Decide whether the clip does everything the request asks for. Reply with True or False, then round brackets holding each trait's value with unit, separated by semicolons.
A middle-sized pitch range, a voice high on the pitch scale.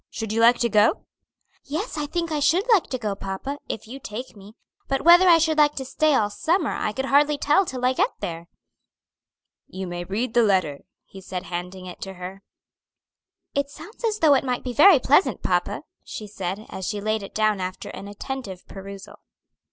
False (7.0 semitones; 235 Hz)